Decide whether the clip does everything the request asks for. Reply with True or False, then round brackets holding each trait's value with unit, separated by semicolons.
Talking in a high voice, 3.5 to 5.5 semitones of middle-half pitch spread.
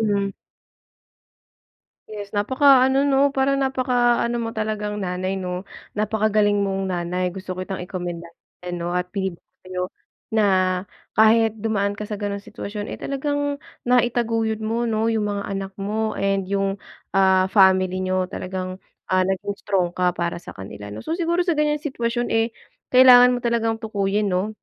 True (205 Hz; 3.8 semitones)